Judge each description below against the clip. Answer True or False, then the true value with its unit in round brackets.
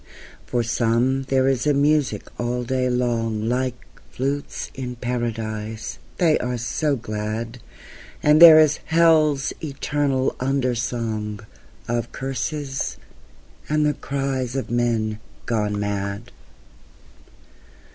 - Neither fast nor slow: False (110 wpm)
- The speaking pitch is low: True (125 Hz)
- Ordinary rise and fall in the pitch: True (3.2 semitones)